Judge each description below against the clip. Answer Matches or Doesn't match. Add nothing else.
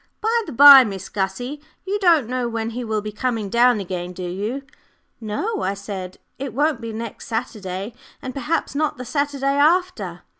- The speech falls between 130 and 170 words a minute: Doesn't match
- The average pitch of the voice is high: Matches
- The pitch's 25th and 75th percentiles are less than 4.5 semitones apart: Doesn't match